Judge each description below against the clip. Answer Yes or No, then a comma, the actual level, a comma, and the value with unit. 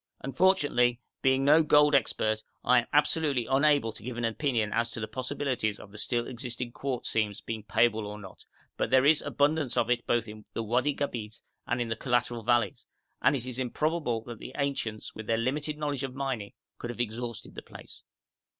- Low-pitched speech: Yes, low, 120 Hz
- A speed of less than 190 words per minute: No, average, 195 wpm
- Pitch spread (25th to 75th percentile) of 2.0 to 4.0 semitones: Yes, average, 3.6 semitones